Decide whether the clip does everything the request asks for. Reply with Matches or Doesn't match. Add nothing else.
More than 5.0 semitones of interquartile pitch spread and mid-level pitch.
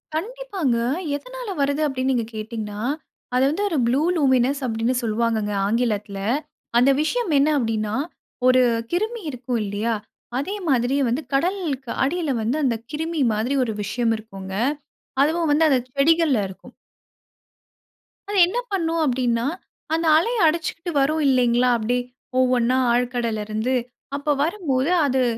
Doesn't match